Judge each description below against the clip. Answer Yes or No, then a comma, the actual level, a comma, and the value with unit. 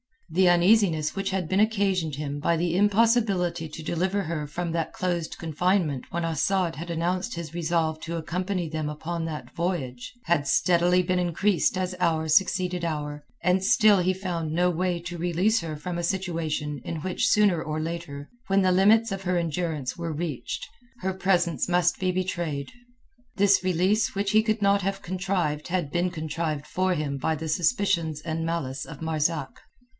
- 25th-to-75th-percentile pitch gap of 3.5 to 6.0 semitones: No, average, 2.9 semitones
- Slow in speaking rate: No, average, 175 wpm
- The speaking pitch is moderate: Yes, medium, 175 Hz